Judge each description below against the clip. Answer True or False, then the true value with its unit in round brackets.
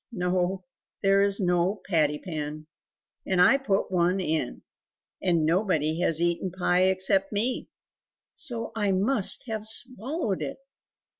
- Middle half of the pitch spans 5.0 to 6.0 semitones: False (3.2 semitones)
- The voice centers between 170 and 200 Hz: True (185 Hz)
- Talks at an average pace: False (130 wpm)